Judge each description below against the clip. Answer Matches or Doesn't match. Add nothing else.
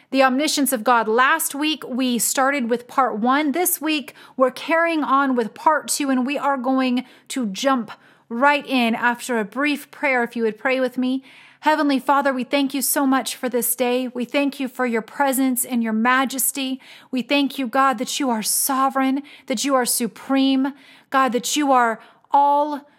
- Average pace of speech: Matches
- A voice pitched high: Matches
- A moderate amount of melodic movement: Doesn't match